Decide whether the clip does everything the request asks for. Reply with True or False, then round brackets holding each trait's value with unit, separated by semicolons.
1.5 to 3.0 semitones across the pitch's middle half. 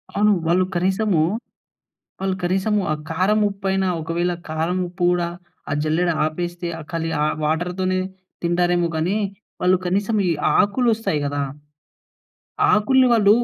True (2.5 semitones)